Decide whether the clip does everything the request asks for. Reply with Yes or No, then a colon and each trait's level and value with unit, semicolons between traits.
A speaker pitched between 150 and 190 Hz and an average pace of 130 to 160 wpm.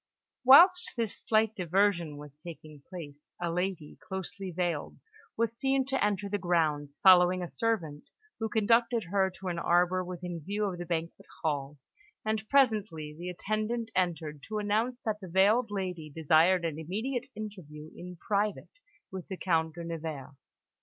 Yes: medium, 185 Hz; average, 155 wpm